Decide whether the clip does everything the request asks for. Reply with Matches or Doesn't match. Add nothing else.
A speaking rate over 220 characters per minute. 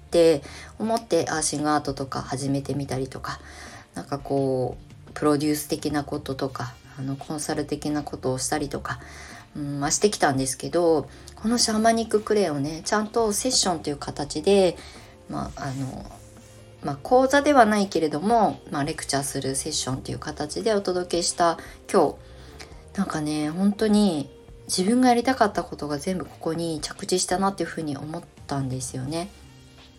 Matches